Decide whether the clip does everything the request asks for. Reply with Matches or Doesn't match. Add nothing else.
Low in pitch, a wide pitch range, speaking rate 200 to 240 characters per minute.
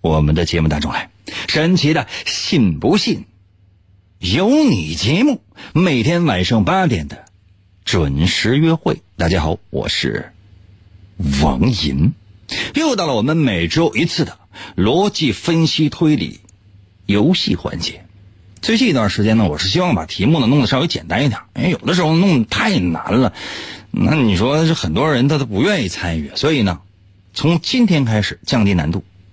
Matches